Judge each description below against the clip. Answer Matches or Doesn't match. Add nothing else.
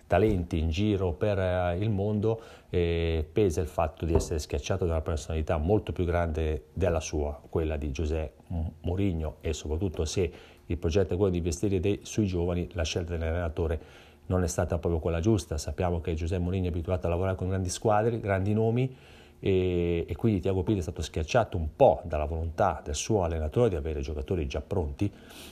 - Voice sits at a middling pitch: Doesn't match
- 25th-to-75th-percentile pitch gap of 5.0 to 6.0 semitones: Doesn't match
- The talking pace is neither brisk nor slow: Doesn't match